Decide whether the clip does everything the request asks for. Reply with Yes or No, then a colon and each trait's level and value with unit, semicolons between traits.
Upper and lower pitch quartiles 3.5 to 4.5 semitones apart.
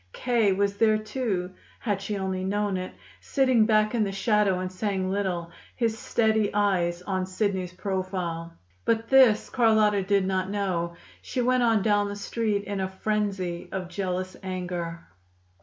No: narrow, 2.6 semitones